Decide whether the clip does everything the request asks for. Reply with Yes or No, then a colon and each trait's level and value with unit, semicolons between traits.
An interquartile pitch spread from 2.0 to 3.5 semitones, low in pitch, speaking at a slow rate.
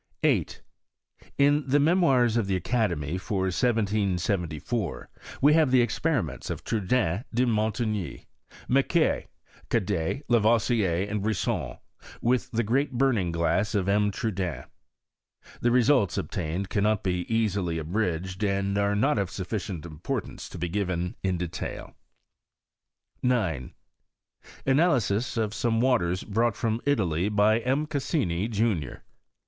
No: average, 4.8 semitones; low, 105 Hz; slow, 125 wpm